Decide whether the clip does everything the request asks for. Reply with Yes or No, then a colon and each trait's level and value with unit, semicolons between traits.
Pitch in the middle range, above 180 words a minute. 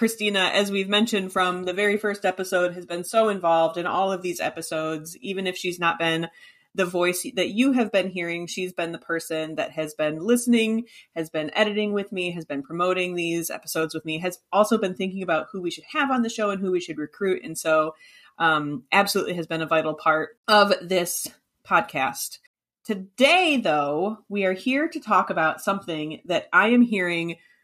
Yes: medium, 180 Hz; average, 200 wpm